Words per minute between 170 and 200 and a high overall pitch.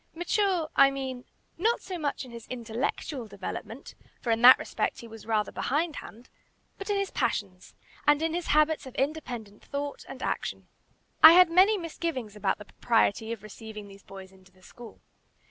Yes: average, 175 wpm; very high, 255 Hz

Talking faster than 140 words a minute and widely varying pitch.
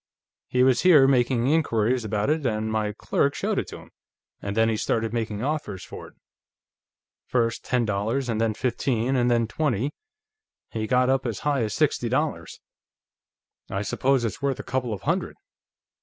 No: average, 175 wpm; average, 3.3 semitones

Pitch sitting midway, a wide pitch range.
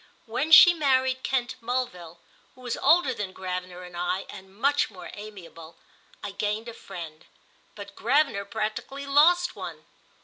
No: high, 215 Hz; wide, 6.3 semitones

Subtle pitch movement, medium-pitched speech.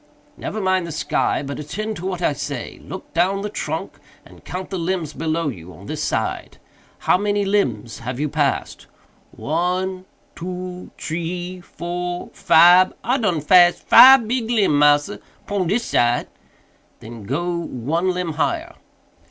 No: average, 3.9 semitones; medium, 175 Hz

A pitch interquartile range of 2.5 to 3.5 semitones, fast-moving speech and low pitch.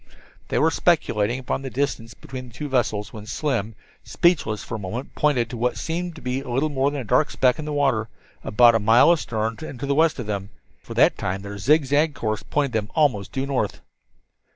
No: average, 4.8 semitones; fast, 225 wpm; low, 125 Hz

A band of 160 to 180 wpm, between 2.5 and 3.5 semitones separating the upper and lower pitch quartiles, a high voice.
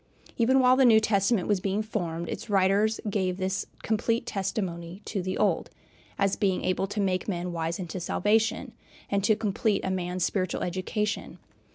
Yes: average, 170 wpm; average, 2.9 semitones; high, 195 Hz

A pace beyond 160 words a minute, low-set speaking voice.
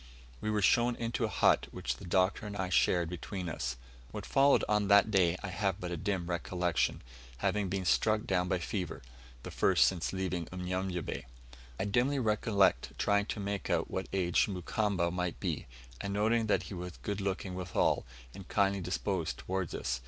Yes: average, 180 wpm; very low, 95 Hz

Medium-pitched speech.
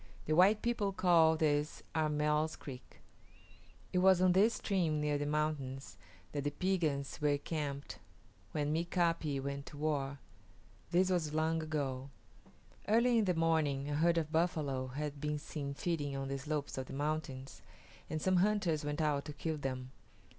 Yes: medium, 150 Hz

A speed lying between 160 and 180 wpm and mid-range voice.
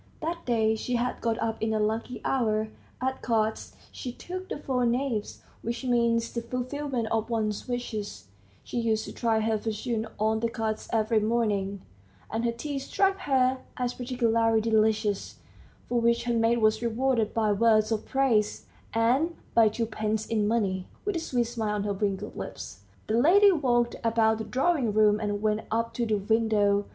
No: average, 175 wpm; high, 230 Hz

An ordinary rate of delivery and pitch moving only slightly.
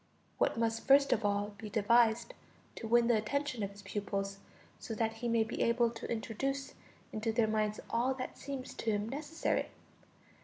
Yes: average, 180 wpm; narrow, 2.3 semitones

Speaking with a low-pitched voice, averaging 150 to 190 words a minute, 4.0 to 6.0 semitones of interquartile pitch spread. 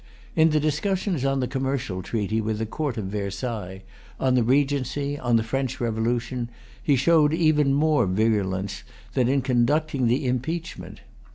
Yes: low, 130 Hz; average, 155 wpm; average, 4.5 semitones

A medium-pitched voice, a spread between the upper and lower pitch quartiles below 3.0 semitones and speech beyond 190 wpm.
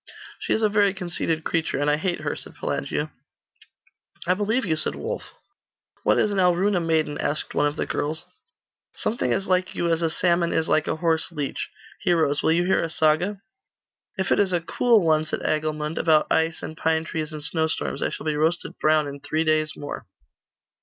Yes: medium, 160 Hz; narrow, 2.6 semitones; average, 200 wpm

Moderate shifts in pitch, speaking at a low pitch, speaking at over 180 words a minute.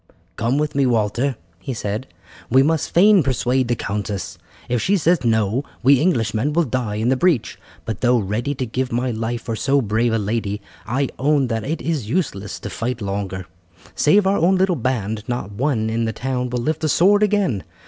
Yes: average, 4.5 semitones; low, 125 Hz; average, 200 wpm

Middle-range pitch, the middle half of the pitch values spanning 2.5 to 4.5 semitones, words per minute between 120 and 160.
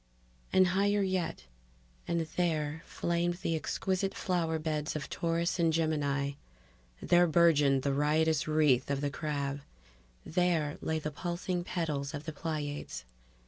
Yes: medium, 160 Hz; average, 2.8 semitones; slow, 135 wpm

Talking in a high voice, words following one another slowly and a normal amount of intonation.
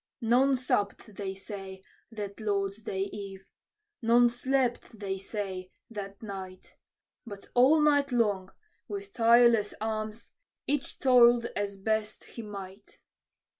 Yes: high, 215 Hz; slow, 120 wpm; average, 3.4 semitones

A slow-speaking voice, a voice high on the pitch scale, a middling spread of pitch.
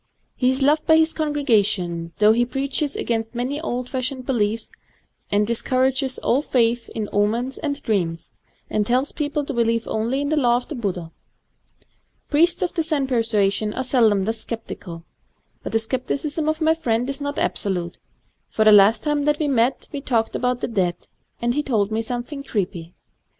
No: average, 185 wpm; high, 240 Hz; average, 4.6 semitones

